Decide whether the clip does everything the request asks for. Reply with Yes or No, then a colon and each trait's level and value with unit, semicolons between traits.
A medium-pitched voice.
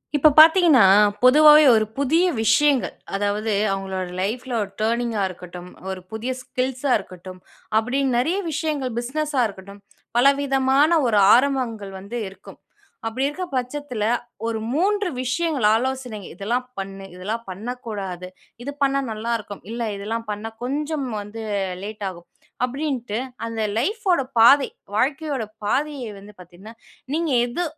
No: high, 240 Hz